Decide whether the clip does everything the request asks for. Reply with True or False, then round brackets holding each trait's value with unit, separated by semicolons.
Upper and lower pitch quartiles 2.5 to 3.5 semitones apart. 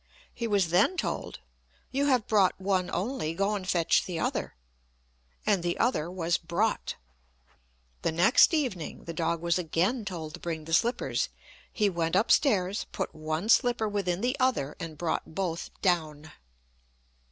False (4.6 semitones)